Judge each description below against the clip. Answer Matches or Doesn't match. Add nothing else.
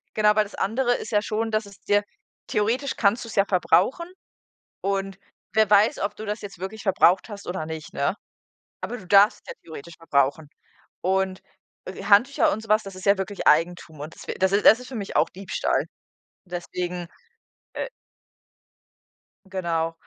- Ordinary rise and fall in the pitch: Matches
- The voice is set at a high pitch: Matches